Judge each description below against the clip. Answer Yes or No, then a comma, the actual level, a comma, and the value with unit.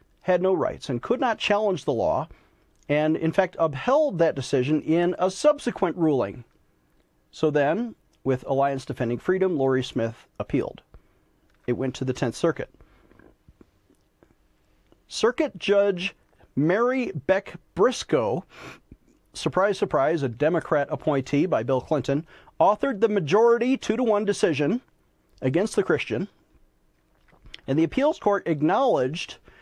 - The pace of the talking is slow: Yes, slow, 125 wpm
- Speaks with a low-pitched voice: No, medium, 160 Hz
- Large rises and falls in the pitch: Yes, wide, 7.0 semitones